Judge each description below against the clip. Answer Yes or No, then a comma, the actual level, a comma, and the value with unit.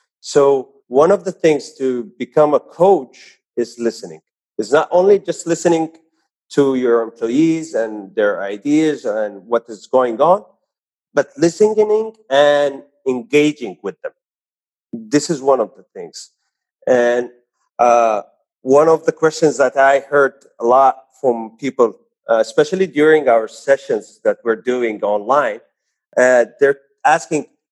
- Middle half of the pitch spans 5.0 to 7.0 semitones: Yes, wide, 5.6 semitones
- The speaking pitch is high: No, medium, 140 Hz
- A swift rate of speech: No, average, 140 wpm